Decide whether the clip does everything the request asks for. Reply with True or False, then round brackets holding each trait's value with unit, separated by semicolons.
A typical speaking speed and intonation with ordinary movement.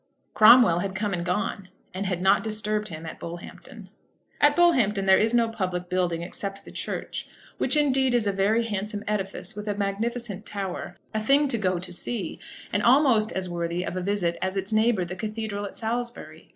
True (190 wpm; 3.5 semitones)